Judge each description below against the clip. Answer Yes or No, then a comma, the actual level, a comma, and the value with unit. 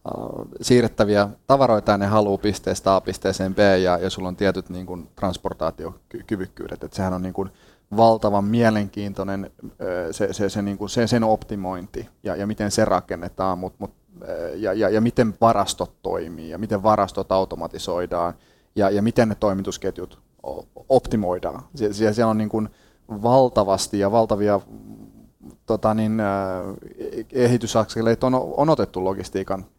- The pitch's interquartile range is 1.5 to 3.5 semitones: Yes, narrow, 2.6 semitones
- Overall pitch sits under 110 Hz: Yes, low, 100 Hz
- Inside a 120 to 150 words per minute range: Yes, average, 135 wpm